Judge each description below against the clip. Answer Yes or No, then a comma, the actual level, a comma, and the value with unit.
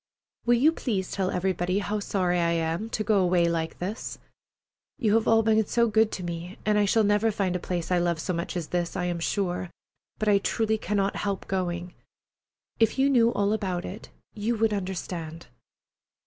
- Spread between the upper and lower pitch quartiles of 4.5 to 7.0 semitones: No, average, 3.5 semitones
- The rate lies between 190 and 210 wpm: Yes, average, 195 wpm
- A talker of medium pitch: No, high, 195 Hz